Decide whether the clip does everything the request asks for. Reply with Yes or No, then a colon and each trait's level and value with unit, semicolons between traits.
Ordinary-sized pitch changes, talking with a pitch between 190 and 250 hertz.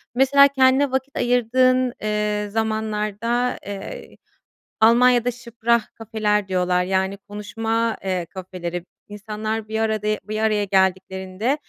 Yes: average, 3.2 semitones; high, 220 Hz